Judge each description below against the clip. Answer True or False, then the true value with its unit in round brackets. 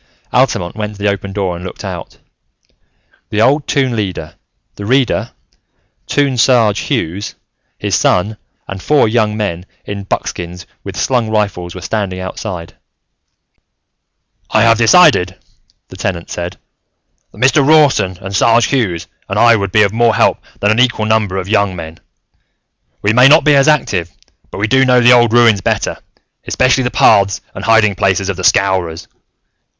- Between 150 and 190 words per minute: True (165 wpm)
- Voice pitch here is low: True (105 Hz)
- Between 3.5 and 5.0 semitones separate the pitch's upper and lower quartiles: True (4.1 semitones)